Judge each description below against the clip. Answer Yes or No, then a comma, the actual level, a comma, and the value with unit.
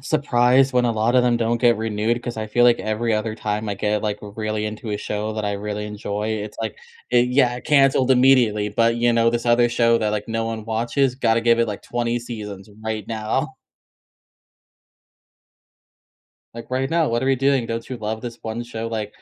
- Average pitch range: No, narrow, 2.1 semitones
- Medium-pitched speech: No, low, 115 Hz